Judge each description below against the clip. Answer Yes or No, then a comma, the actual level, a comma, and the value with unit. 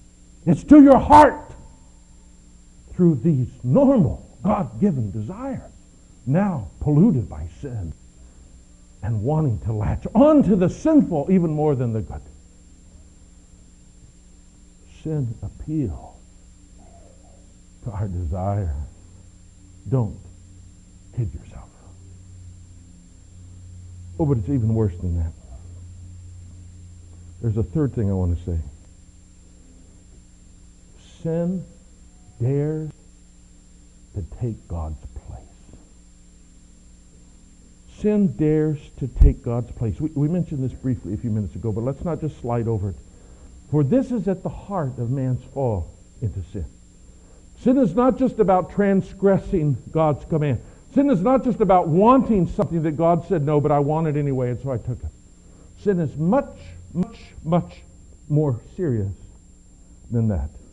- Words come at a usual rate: No, slow, 125 wpm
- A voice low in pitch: Yes, low, 100 Hz